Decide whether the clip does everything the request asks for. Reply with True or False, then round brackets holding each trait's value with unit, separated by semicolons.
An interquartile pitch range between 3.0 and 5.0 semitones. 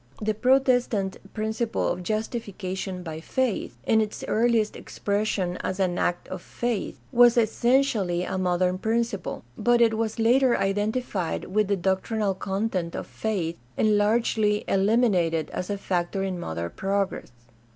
True (3.5 semitones)